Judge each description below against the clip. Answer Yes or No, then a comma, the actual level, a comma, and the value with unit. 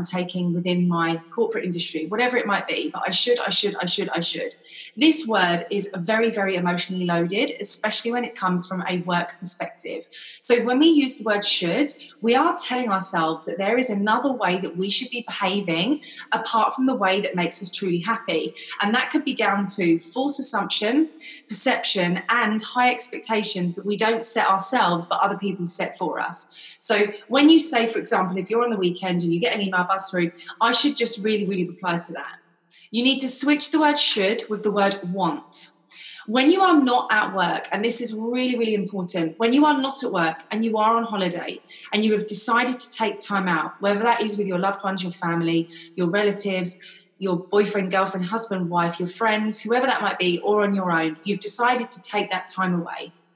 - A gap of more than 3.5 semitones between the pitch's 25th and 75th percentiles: Yes, average, 4.8 semitones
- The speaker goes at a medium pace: No, fast, 210 wpm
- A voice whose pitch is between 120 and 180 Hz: No, high, 205 Hz